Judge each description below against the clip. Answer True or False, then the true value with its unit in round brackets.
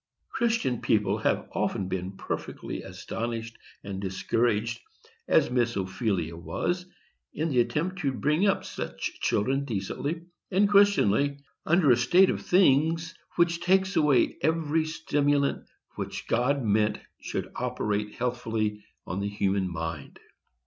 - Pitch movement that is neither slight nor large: False (7.6 semitones)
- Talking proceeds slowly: True (130 wpm)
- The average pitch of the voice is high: False (125 Hz)